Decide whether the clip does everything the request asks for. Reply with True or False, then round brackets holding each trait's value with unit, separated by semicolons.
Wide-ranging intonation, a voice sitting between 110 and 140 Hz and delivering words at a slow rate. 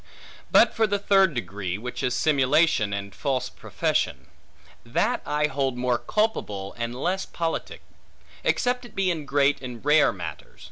False (6.2 semitones; 135 Hz; 150 wpm)